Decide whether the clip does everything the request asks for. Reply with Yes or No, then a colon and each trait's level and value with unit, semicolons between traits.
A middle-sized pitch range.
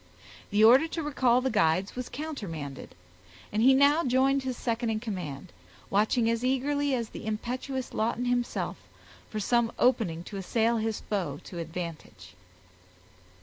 Yes: average, 4.6 semitones